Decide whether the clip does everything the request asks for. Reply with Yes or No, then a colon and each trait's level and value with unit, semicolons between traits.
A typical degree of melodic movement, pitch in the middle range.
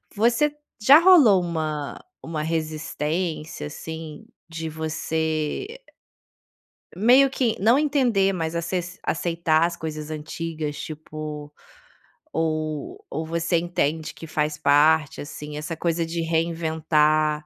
No: narrow, 2.3 semitones; medium, 160 Hz